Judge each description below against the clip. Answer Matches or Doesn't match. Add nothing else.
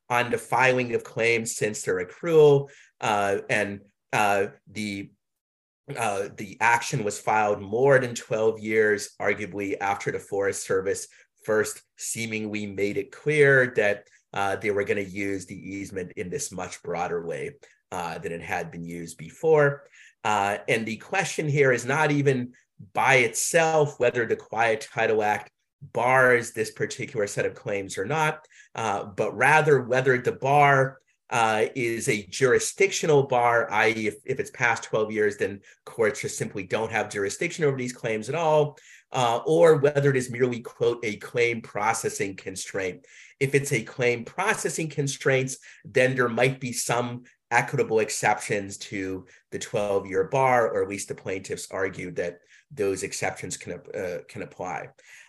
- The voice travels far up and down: Matches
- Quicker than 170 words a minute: Doesn't match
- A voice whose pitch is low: Matches